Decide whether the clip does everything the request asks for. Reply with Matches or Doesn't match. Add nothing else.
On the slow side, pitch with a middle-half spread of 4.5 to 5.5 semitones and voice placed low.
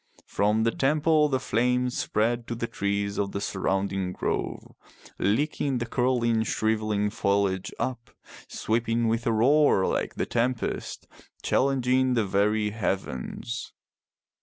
Doesn't match